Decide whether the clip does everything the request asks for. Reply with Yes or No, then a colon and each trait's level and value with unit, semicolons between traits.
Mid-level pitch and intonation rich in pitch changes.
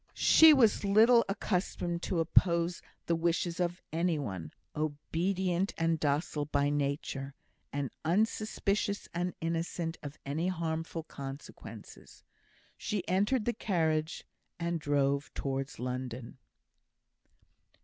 No: medium, 165 Hz; average, 4.0 semitones